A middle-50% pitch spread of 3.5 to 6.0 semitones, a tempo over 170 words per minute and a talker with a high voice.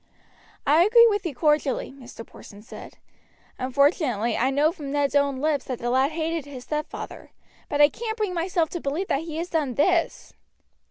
Yes: average, 3.9 semitones; average, 180 wpm; very high, 295 Hz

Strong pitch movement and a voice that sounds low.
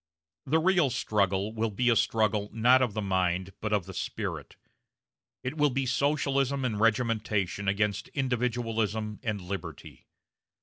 No: average, 3.9 semitones; low, 110 Hz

